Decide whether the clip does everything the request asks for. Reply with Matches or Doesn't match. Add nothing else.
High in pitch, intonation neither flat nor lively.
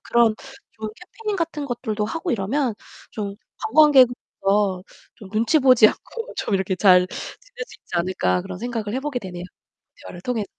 Doesn't match